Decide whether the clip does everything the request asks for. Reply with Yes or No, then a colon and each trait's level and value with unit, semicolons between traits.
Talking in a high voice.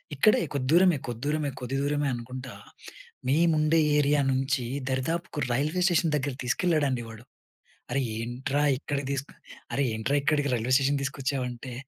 No: medium, 140 Hz